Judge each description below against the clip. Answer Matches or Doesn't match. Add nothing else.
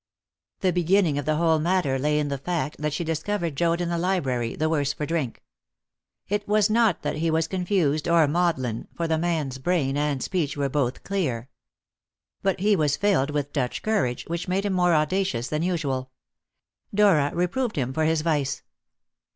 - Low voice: Doesn't match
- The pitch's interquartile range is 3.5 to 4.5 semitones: Matches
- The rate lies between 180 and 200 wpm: Matches